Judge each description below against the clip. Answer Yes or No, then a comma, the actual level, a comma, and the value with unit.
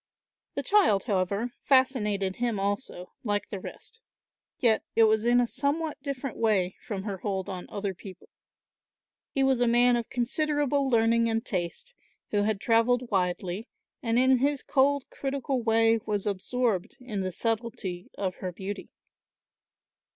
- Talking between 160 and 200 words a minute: No, average, 150 wpm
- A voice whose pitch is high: Yes, high, 225 Hz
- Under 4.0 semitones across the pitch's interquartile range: No, average, 4.3 semitones